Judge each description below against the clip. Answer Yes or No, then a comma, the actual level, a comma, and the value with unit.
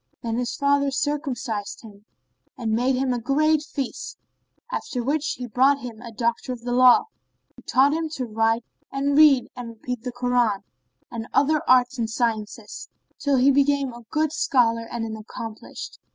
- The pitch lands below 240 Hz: No, very high, 250 Hz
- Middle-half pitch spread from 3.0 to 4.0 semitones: Yes, average, 3.5 semitones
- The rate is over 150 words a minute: Yes, average, 170 wpm